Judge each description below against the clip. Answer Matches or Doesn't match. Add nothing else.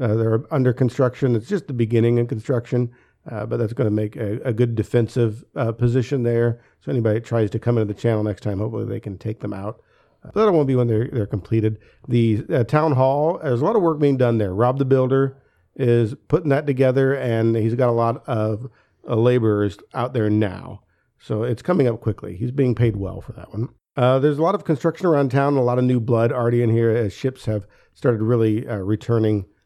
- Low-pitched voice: Matches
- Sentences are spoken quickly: Matches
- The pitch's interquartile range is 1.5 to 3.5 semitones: Matches